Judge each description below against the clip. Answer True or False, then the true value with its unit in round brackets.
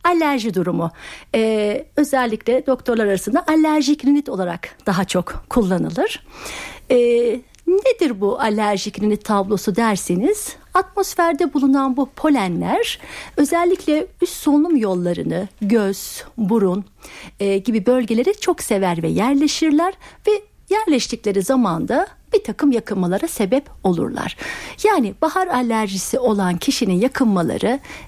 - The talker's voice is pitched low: False (245 Hz)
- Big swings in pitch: True (6.8 semitones)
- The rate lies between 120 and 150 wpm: False (105 wpm)